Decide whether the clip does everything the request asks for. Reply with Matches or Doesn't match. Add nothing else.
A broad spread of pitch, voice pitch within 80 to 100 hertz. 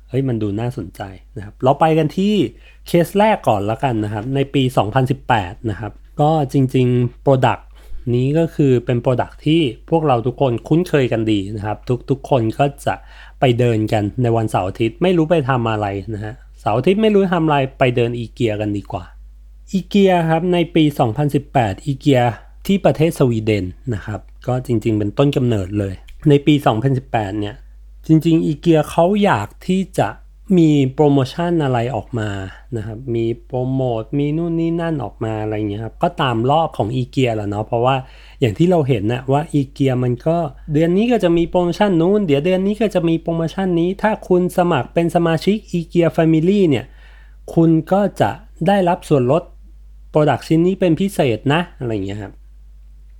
Doesn't match